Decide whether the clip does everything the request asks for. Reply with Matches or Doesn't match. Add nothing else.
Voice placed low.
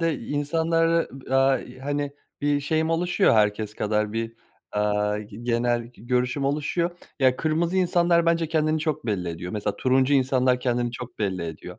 Matches